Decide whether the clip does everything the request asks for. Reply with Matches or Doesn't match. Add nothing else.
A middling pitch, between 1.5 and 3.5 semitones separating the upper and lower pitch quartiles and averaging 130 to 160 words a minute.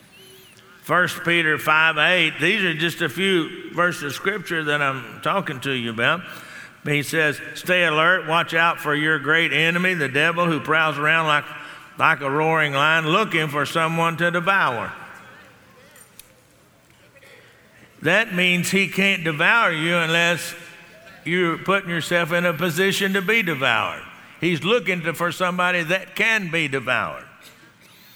Matches